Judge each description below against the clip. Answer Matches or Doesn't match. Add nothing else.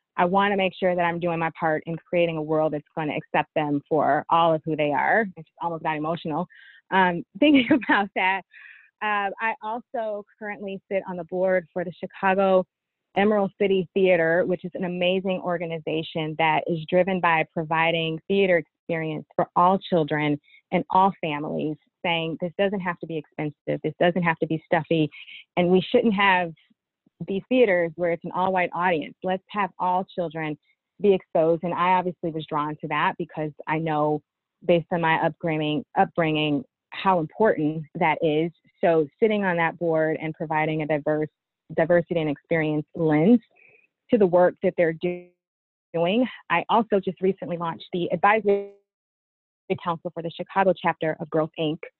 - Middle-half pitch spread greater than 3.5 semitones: Doesn't match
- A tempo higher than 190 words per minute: Doesn't match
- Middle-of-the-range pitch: Matches